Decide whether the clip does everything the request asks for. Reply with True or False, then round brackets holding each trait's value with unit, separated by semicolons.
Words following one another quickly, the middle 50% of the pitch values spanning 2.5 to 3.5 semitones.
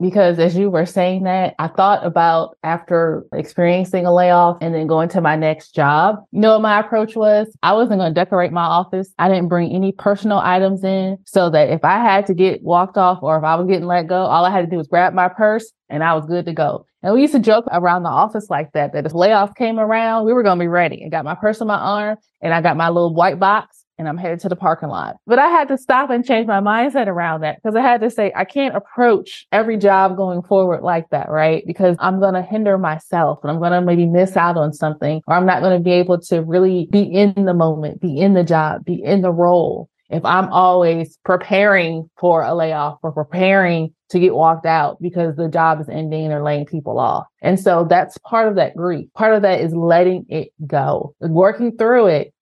True (245 wpm; 3.2 semitones)